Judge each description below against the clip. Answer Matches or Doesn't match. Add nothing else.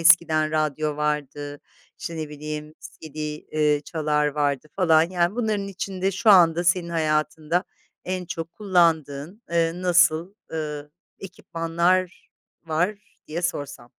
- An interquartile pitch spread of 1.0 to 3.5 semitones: Matches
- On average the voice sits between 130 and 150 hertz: Doesn't match